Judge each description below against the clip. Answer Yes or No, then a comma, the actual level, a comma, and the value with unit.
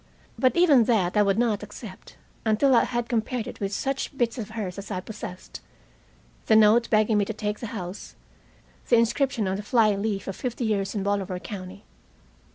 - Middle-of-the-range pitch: No, high, 215 Hz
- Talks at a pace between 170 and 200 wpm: Yes, average, 190 wpm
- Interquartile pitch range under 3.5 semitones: Yes, average, 2.9 semitones